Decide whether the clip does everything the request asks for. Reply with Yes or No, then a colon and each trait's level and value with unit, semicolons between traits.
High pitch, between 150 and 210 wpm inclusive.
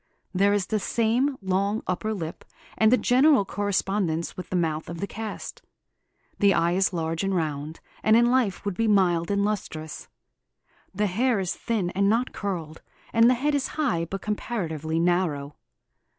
Yes: high, 195 Hz; average, 170 wpm